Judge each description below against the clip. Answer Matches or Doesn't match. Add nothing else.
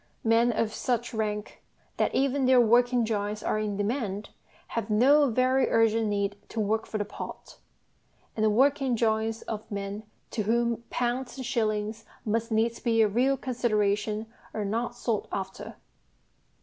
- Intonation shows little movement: Matches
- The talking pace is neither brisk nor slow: Matches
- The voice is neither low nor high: Doesn't match